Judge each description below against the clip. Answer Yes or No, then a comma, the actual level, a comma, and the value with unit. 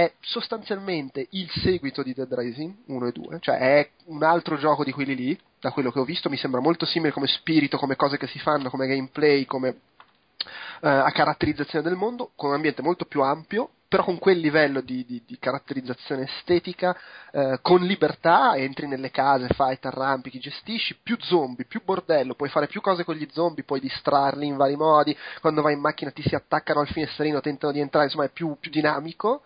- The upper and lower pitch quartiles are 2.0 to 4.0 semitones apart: Yes, average, 3.7 semitones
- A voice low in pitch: No, medium, 150 Hz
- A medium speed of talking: No, fast, 205 wpm